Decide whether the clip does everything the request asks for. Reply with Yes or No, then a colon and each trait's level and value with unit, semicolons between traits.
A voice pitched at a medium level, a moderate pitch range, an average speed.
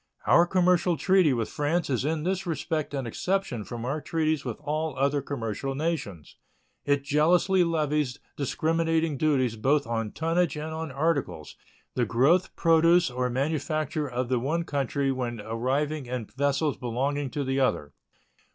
Yes: medium, 145 Hz; average, 4.1 semitones; average, 150 wpm